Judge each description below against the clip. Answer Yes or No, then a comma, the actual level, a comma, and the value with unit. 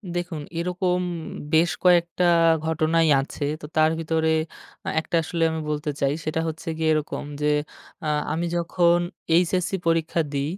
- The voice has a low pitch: No, medium, 165 Hz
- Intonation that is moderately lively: No, narrow, 1.7 semitones